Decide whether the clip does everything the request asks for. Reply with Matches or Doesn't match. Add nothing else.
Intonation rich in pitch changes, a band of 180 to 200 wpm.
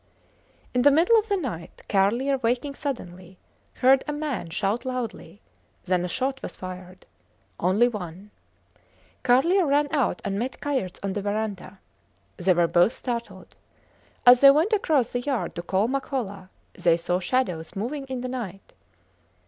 Doesn't match